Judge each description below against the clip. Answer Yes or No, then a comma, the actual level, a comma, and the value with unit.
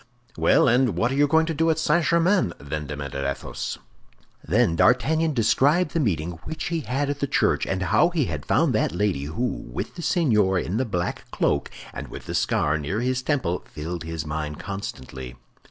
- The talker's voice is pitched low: Yes, low, 110 Hz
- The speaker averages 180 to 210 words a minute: Yes, average, 195 wpm